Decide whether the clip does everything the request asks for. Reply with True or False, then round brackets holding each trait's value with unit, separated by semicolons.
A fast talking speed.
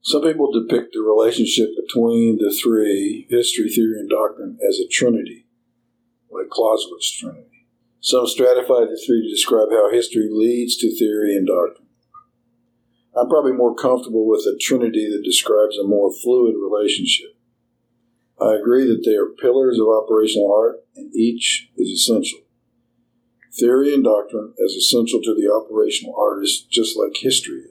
False (150 wpm)